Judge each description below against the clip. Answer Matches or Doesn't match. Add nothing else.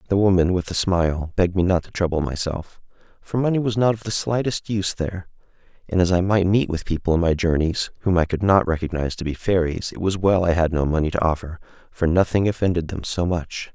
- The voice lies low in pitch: Matches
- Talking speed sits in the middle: Doesn't match